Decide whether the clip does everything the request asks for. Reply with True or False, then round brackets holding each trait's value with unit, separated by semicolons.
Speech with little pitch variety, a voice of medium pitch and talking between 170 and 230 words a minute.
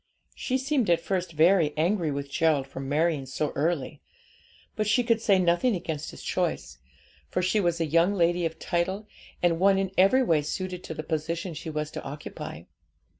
False (3.8 semitones; 170 Hz; 185 wpm)